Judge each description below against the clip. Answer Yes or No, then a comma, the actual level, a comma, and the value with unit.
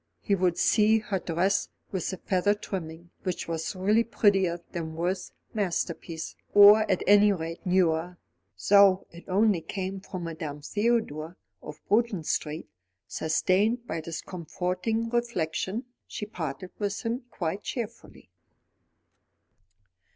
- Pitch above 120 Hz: Yes, medium, 185 Hz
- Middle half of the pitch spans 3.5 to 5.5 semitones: Yes, average, 3.8 semitones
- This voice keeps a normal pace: No, slow, 125 wpm